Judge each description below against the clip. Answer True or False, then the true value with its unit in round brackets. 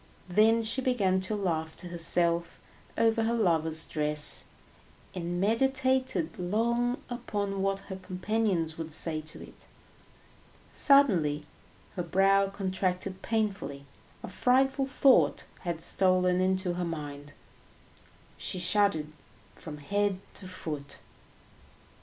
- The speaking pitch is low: False (185 Hz)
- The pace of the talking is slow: True (110 wpm)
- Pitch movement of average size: True (4.7 semitones)